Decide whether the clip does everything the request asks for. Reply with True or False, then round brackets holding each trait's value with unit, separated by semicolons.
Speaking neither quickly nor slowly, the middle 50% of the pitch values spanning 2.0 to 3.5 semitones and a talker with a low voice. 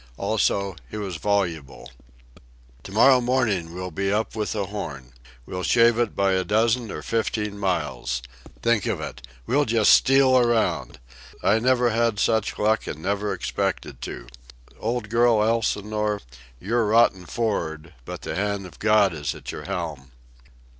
False (155 wpm; 3.9 semitones; 105 Hz)